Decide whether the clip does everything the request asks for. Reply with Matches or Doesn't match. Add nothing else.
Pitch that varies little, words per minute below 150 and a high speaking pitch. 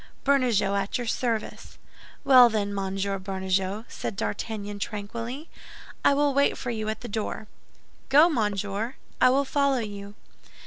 Doesn't match